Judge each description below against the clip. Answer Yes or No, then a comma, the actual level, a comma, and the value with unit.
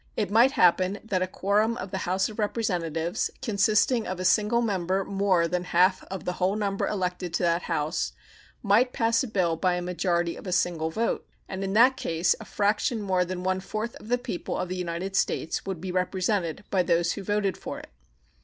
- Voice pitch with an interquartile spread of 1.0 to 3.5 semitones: Yes, narrow, 2.6 semitones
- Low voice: No, high, 190 Hz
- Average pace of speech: No, fast, 210 wpm